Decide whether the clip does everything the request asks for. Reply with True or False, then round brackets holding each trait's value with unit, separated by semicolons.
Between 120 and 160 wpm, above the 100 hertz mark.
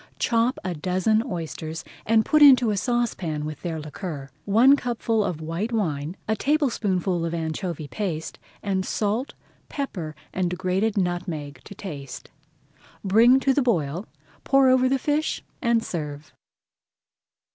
True (135 wpm; 190 Hz)